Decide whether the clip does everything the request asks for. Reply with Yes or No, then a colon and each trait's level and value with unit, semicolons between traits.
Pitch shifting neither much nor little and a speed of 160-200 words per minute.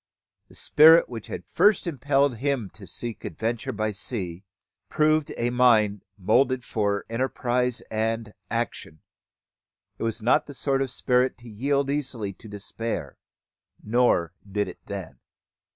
No: average, 4.0 semitones; slow, 135 wpm